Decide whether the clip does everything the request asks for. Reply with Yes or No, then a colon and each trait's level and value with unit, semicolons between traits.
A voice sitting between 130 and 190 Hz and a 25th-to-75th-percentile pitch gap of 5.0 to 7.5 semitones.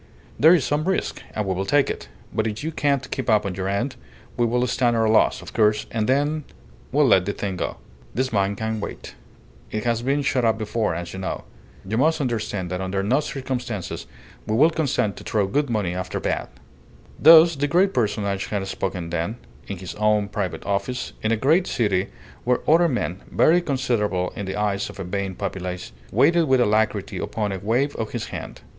No: low, 110 Hz; average, 5.3 semitones